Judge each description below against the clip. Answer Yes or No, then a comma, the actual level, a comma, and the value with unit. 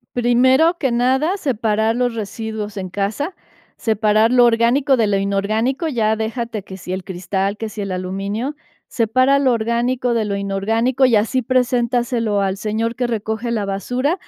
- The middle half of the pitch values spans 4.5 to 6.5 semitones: No, average, 3.4 semitones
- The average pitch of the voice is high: Yes, high, 230 Hz